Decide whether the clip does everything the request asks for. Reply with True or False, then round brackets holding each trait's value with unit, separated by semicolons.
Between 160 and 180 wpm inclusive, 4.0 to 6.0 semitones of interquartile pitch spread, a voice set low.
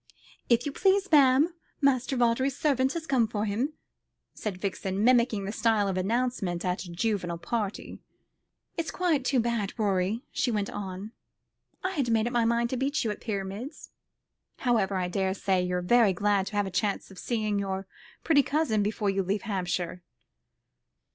False (170 wpm; 4.7 semitones; 215 Hz)